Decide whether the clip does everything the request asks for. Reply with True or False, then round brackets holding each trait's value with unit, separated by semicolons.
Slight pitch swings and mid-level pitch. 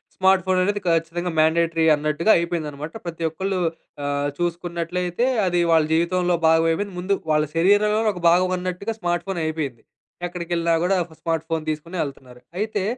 True (2.2 semitones; 170 Hz)